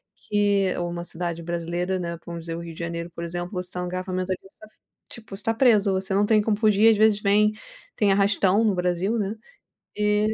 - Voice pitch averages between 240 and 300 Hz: No, high, 190 Hz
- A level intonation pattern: No, average, 3.1 semitones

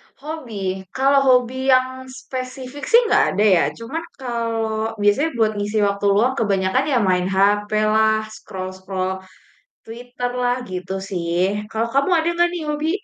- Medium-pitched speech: No, high, 220 Hz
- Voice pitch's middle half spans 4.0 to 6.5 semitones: Yes, average, 4.7 semitones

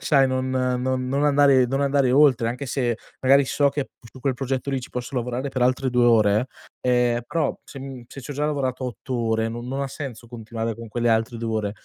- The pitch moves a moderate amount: No, narrow, 2.3 semitones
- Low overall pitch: Yes, low, 130 Hz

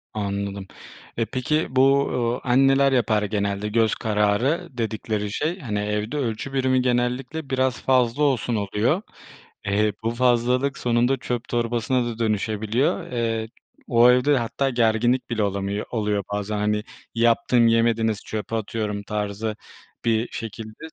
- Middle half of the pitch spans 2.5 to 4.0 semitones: Yes, average, 3.2 semitones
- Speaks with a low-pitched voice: Yes, low, 115 Hz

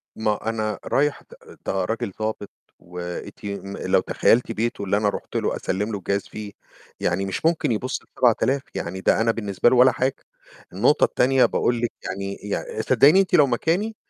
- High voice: No, low, 110 Hz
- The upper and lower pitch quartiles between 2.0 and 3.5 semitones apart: No, average, 4.4 semitones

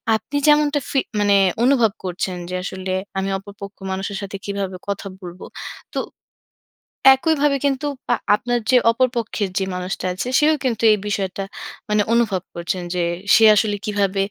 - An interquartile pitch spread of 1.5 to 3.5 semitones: No, average, 4.2 semitones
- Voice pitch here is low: No, high, 205 Hz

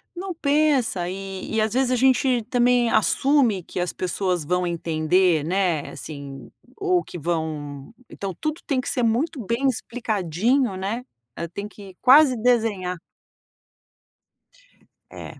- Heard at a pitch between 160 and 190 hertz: No, high, 215 Hz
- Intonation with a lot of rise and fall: Yes, wide, 6.2 semitones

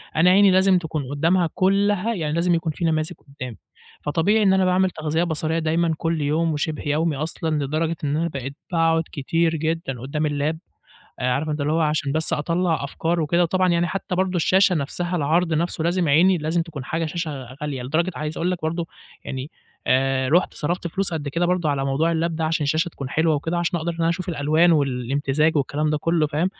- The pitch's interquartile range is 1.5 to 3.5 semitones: Yes, average, 2.7 semitones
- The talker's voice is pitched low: No, medium, 160 Hz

